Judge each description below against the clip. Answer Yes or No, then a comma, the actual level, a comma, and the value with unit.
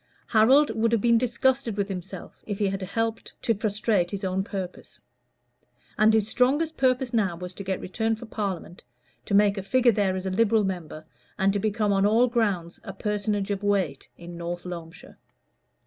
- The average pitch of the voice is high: Yes, high, 205 Hz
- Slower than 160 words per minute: No, average, 185 wpm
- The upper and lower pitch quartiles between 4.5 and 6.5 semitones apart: No, average, 3.2 semitones